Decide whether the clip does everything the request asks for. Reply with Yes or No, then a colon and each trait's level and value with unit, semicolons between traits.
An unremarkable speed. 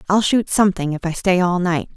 No: fast, 245 wpm